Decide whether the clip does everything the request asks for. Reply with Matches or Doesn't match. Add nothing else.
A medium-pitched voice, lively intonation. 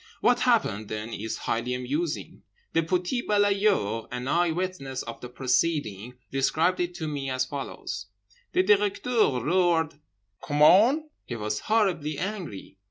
Matches